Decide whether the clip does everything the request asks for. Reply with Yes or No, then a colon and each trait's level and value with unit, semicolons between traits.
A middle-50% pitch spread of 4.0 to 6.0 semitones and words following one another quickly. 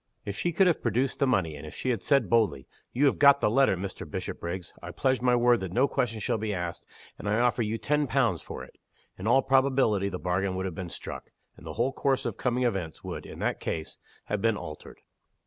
Yes: wide, 5.5 semitones; fast, 235 wpm